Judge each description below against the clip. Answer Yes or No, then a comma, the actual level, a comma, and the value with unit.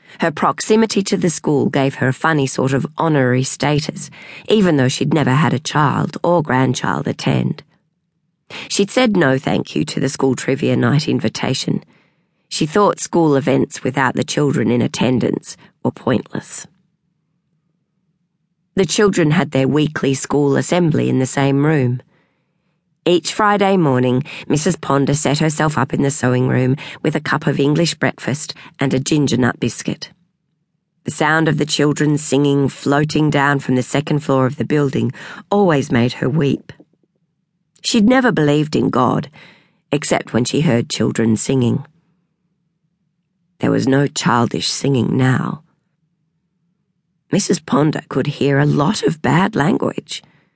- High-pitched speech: No, medium, 155 Hz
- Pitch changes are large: No, average, 4.1 semitones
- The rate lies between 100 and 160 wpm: Yes, average, 145 wpm